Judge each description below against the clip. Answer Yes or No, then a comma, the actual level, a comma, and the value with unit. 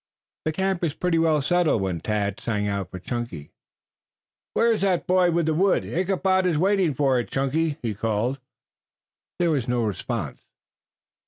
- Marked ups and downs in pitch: Yes, wide, 8.0 semitones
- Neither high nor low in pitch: Yes, medium, 150 Hz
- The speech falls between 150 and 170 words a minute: Yes, average, 165 wpm